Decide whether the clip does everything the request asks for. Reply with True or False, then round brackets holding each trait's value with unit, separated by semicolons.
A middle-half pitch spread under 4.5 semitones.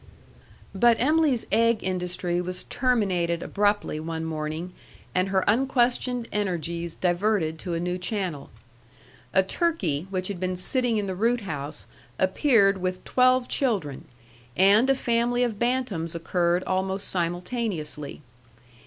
False (5.3 semitones)